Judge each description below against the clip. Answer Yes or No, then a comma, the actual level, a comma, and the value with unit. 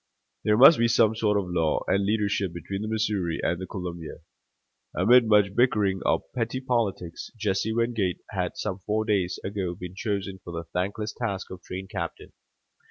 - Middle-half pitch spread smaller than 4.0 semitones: Yes, average, 3.2 semitones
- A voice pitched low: Yes, low, 100 Hz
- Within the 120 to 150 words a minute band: No, average, 170 wpm